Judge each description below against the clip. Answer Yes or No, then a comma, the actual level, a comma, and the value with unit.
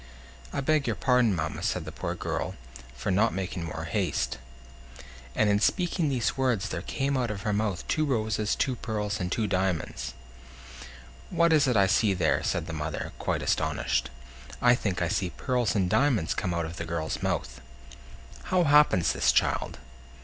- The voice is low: Yes, low, 105 Hz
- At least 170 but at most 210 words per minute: Yes, average, 180 wpm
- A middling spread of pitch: No, wide, 6.3 semitones